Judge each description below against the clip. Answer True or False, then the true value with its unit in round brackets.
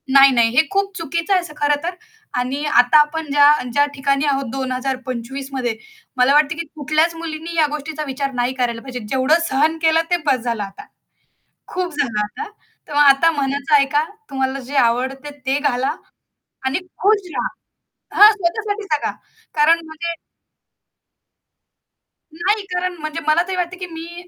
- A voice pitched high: True (295 Hz)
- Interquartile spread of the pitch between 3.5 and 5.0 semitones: True (3.8 semitones)